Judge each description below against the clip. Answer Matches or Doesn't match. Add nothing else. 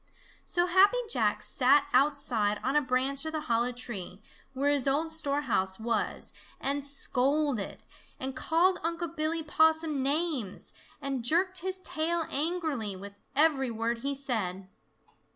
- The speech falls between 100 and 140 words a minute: Matches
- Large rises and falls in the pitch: Doesn't match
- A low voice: Doesn't match